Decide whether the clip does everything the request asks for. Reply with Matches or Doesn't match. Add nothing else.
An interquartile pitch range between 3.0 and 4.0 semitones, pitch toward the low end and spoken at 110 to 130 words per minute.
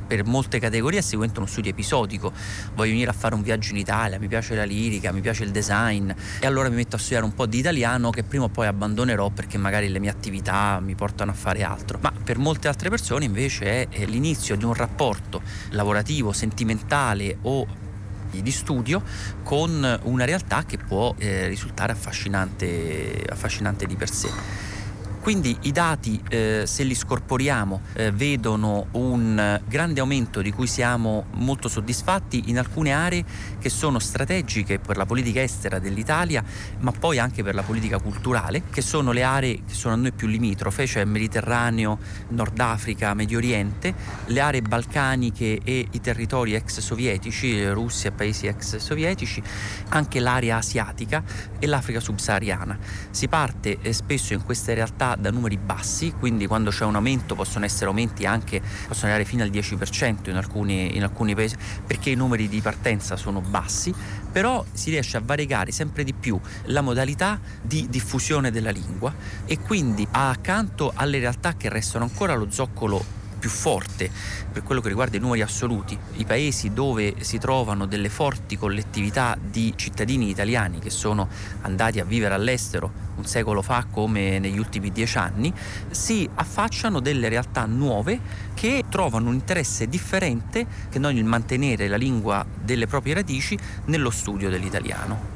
Doesn't match